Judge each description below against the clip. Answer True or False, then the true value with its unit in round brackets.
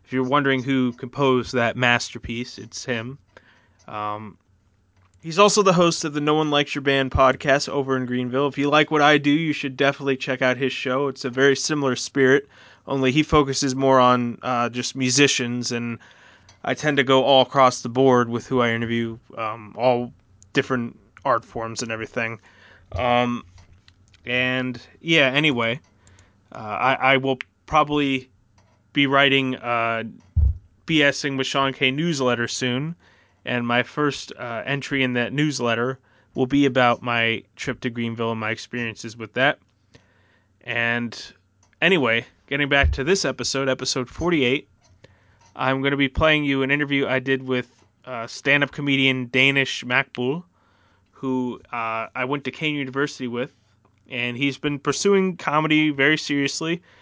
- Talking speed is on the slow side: False (155 wpm)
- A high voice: False (130 Hz)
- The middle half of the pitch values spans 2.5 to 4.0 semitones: True (3.3 semitones)